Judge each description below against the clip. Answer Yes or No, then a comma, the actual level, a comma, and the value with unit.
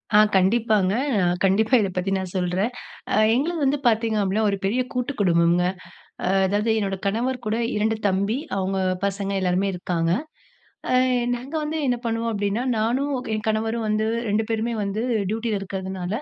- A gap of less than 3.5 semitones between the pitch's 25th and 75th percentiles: Yes, average, 3.0 semitones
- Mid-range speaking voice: No, high, 210 Hz